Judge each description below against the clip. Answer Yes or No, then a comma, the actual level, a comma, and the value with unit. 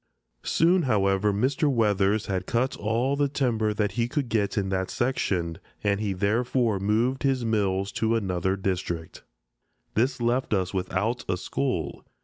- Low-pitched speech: Yes, low, 105 Hz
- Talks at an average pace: Yes, average, 150 wpm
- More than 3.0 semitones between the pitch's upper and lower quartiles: Yes, average, 4.2 semitones